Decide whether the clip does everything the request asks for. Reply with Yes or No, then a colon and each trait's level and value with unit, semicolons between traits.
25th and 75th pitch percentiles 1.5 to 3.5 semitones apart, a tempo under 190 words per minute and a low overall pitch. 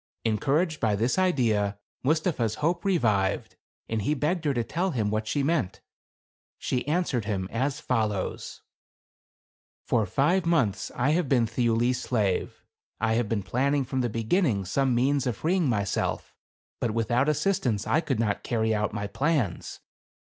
No: wide, 5.6 semitones; average, 160 wpm; low, 125 Hz